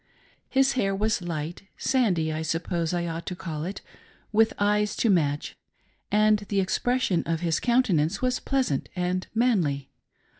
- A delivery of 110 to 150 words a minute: No, average, 165 wpm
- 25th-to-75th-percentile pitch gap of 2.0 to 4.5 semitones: No, average, 5.0 semitones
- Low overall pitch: No, medium, 185 Hz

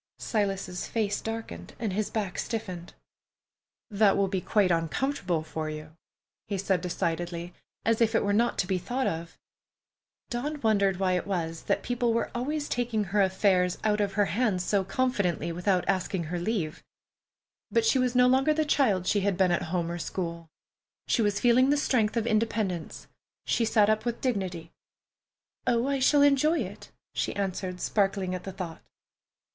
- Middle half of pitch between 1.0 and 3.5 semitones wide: No, average, 4.5 semitones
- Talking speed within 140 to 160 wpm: No, average, 175 wpm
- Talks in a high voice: Yes, high, 200 Hz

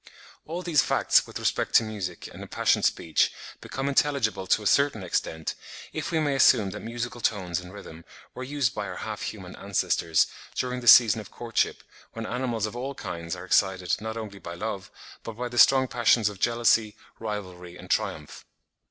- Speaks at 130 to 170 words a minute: No, average, 185 wpm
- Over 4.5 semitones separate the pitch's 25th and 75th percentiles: Yes, average, 4.9 semitones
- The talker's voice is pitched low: Yes, low, 110 Hz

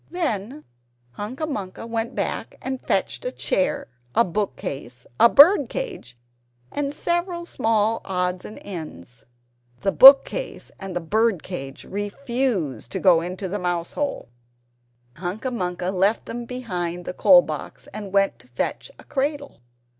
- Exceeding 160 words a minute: No, average, 145 wpm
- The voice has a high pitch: Yes, high, 205 Hz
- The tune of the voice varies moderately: No, wide, 6.9 semitones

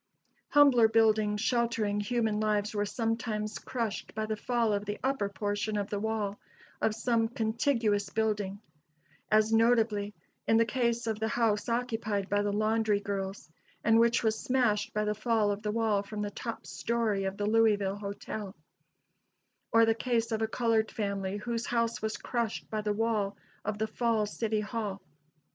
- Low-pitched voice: No, high, 220 Hz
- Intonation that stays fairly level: Yes, narrow, 1.8 semitones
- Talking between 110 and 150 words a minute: No, average, 170 wpm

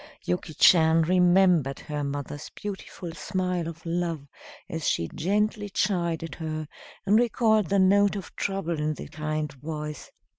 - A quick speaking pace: No, average, 140 wpm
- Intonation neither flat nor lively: Yes, average, 3.9 semitones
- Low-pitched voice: No, medium, 170 Hz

